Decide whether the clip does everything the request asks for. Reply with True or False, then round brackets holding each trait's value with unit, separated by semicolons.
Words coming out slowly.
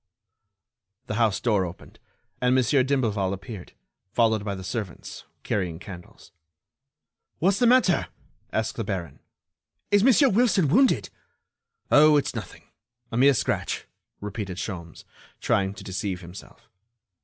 True (120 wpm)